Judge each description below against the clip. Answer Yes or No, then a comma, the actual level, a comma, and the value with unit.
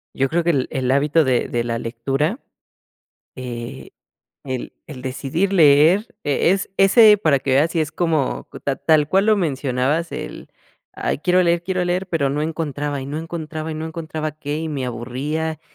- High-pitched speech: No, medium, 155 Hz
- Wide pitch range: No, average, 3.8 semitones